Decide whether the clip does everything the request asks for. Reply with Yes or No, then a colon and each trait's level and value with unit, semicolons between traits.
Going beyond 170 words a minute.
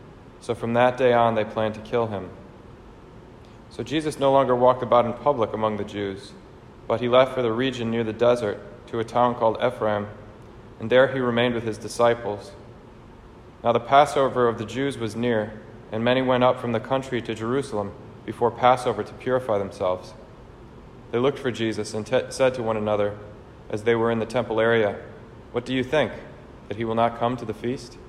Yes: average, 200 wpm